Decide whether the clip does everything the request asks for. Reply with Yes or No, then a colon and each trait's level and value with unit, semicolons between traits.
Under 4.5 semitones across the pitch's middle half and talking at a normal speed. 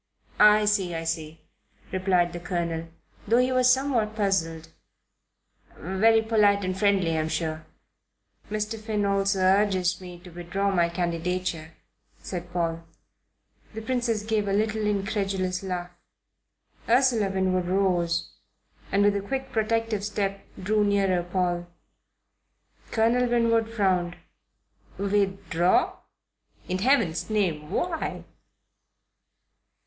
No: average, 3.5 semitones; slow, 115 wpm